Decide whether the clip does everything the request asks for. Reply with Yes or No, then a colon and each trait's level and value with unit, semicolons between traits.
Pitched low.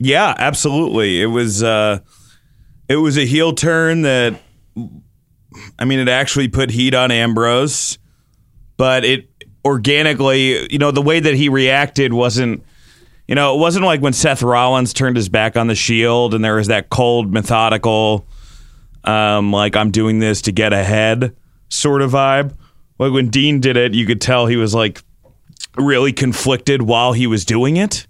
Yes: low, 125 Hz